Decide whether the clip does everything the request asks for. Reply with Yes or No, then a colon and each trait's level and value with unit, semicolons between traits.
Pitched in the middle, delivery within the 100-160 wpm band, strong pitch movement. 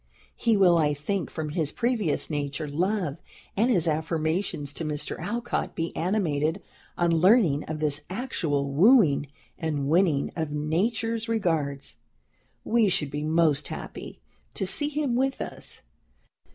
Yes: medium, 165 Hz; average, 140 wpm; wide, 5.7 semitones